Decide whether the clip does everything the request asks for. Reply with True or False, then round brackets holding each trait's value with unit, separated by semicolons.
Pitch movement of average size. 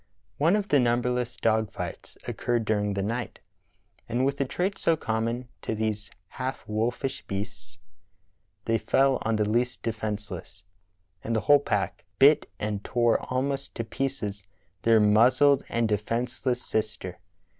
True (3.1 semitones)